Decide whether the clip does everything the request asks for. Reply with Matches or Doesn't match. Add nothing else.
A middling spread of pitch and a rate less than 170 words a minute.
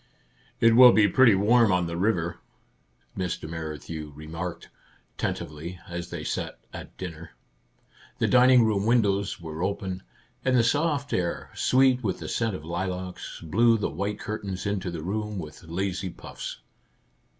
Matches